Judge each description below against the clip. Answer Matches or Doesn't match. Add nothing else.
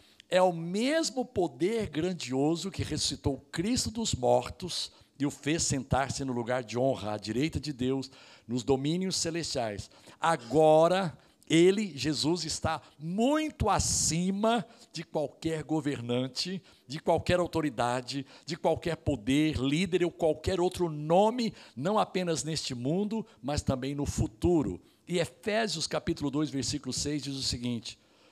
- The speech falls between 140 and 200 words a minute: Doesn't match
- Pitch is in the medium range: Matches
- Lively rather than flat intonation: Doesn't match